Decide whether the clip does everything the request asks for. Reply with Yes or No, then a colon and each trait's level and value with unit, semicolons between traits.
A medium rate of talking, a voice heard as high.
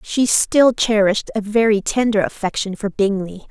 Yes: average, 155 wpm; high, 210 Hz